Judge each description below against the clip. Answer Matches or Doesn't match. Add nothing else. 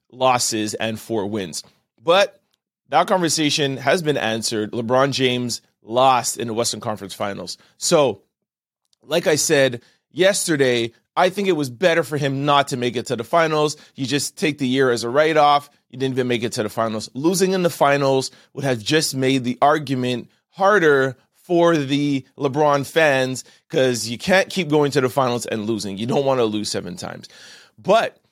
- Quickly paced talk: Doesn't match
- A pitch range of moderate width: Matches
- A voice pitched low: Matches